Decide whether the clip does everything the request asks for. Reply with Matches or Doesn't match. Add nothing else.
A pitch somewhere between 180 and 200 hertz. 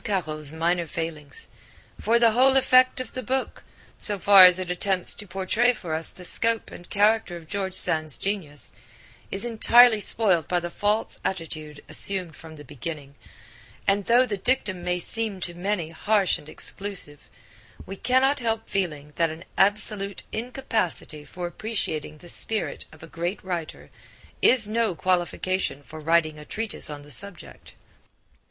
Matches